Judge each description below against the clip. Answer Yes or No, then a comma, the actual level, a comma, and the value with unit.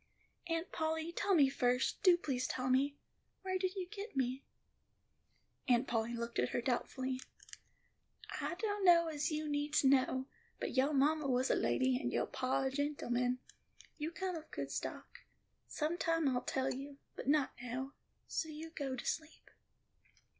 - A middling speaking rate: Yes, average, 165 wpm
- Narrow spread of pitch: No, average, 4.0 semitones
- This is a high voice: Yes, very high, 280 Hz